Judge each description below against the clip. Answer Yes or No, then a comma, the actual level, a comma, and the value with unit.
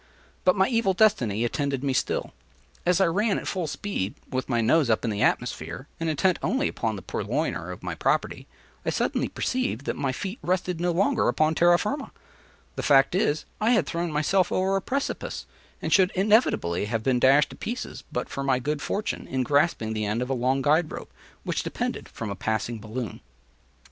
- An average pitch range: No, wide, 7.4 semitones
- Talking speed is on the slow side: No, average, 200 wpm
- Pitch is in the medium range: Yes, medium, 150 Hz